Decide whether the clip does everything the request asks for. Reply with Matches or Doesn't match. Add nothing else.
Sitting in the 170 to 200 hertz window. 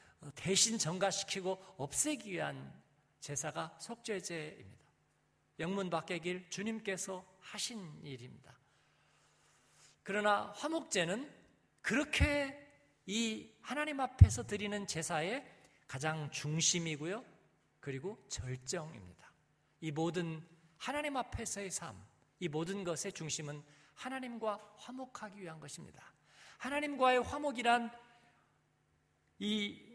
Matches